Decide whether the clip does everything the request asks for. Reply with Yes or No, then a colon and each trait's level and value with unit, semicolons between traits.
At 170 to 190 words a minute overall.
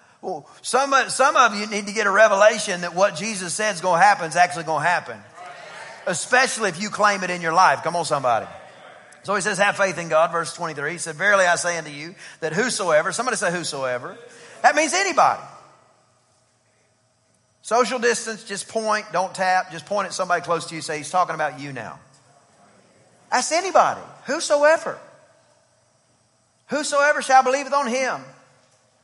Yes: average, 180 wpm